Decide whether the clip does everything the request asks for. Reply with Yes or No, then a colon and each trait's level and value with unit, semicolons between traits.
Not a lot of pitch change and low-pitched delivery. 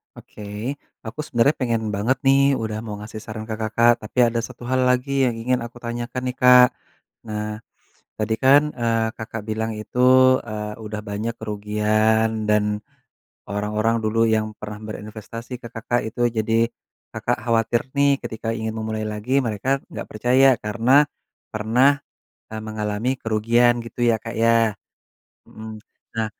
Yes: narrow, 2.0 semitones; low, 115 Hz